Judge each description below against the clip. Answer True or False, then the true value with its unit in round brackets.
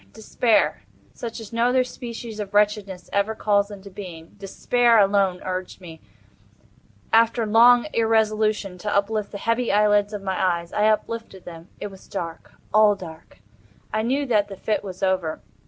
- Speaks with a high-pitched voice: True (205 Hz)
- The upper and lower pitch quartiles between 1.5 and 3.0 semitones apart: True (2.7 semitones)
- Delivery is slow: False (150 wpm)